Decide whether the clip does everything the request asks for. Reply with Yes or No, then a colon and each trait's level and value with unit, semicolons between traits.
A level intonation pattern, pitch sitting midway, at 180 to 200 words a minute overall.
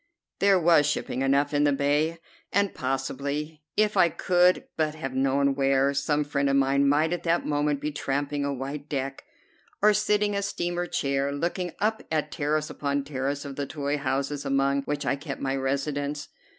Yes: narrow, 2.2 semitones; medium, 145 Hz; average, 185 wpm